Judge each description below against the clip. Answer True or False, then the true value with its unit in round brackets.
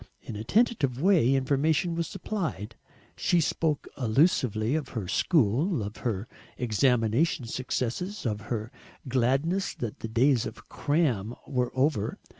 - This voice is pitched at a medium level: False (130 Hz)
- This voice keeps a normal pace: False (130 wpm)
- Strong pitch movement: True (5.9 semitones)